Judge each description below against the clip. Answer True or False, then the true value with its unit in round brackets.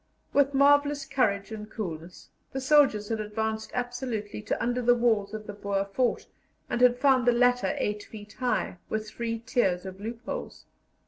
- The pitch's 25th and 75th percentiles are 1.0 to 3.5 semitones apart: True (3.2 semitones)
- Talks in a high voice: True (230 Hz)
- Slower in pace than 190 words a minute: True (170 wpm)